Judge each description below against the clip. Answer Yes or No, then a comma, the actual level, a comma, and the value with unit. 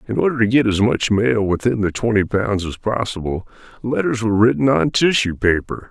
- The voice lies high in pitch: No, low, 110 Hz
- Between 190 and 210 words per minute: Yes, average, 195 wpm